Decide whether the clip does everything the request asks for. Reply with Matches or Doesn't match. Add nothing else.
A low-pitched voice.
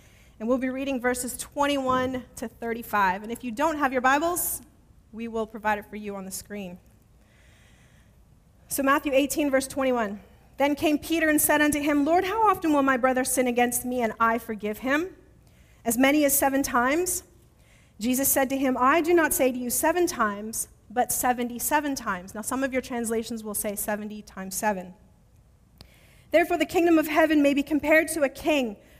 Doesn't match